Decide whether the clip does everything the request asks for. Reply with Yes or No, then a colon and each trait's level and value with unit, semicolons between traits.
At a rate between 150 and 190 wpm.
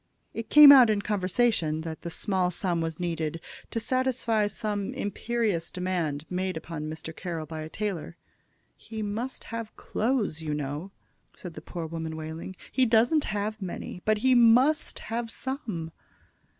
Yes: average, 155 wpm